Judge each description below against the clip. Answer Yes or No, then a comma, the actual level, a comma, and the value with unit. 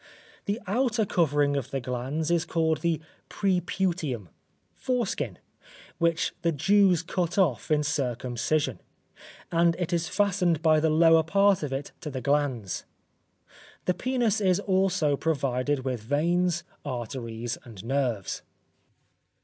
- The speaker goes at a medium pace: No, slow, 125 wpm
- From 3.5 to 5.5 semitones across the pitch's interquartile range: Yes, average, 5.1 semitones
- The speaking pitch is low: No, medium, 160 Hz